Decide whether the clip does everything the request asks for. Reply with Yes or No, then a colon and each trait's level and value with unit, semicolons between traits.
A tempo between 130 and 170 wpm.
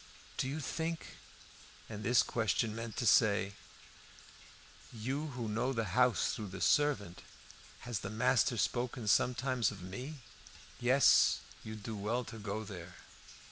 Yes: average, 140 wpm